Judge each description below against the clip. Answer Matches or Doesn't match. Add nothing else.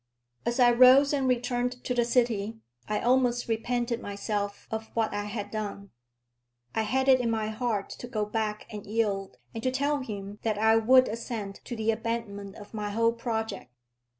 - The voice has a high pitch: Matches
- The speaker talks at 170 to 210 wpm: Matches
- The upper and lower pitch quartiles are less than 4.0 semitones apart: Matches